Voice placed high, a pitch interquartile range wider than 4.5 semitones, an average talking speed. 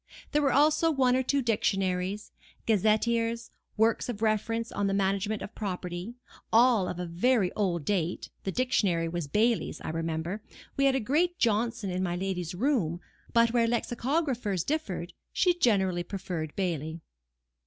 Yes: high, 210 Hz; average, 5.0 semitones; average, 155 wpm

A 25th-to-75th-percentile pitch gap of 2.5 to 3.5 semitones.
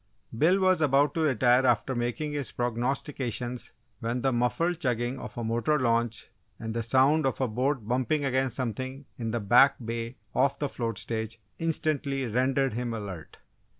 Yes: average, 3.0 semitones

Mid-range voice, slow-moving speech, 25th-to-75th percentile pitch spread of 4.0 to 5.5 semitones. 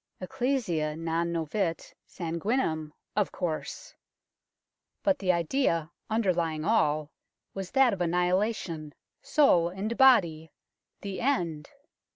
Yes: medium, 175 Hz; slow, 100 wpm; average, 5.2 semitones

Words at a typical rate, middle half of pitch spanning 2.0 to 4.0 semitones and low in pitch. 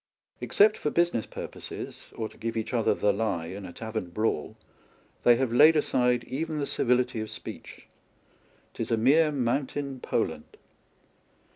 No: average, 150 wpm; average, 4.4 semitones; low, 120 Hz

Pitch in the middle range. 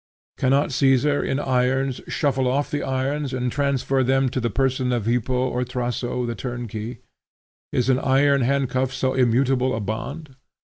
No: low, 130 Hz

